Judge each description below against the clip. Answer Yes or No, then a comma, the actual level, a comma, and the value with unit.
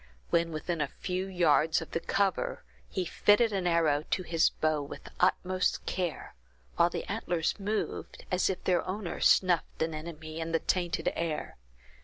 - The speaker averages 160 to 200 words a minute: Yes, average, 170 wpm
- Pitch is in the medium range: Yes, medium, 170 Hz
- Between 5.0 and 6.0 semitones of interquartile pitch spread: No, narrow, 2.5 semitones